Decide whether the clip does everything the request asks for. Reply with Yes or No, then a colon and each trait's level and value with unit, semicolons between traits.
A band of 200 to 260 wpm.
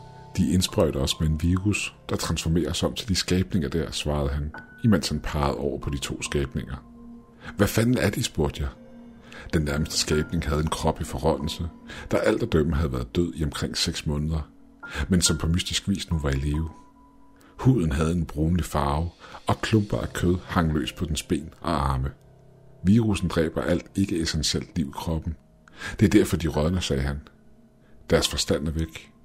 No: average, 190 wpm